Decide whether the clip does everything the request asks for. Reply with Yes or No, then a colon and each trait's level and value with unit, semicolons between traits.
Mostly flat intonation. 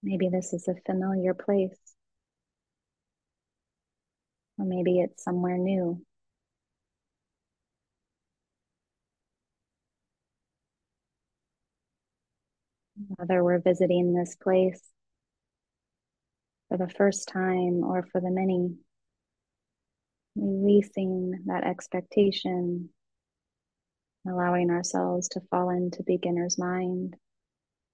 Yes: narrow, 1.0 semitones